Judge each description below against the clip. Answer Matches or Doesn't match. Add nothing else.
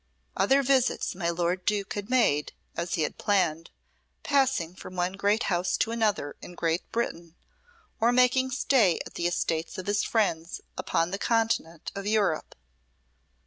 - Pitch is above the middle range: Matches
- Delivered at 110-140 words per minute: Doesn't match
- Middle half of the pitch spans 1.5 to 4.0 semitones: Doesn't match